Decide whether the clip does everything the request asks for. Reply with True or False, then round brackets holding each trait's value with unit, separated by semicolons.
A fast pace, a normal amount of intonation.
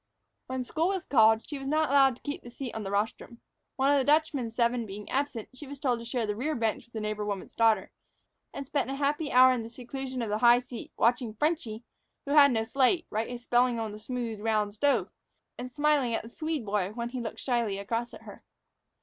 True (235 wpm; 3.7 semitones)